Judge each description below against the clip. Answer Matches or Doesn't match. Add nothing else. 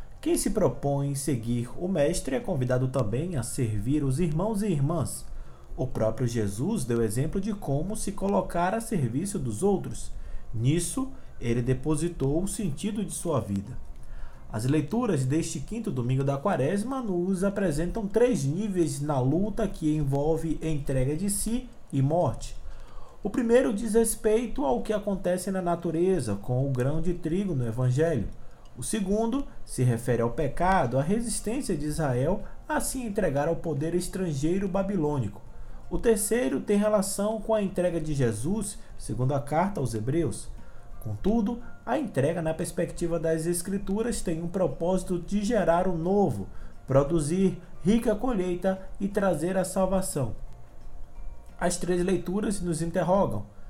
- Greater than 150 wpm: Doesn't match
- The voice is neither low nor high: Matches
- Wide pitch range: Matches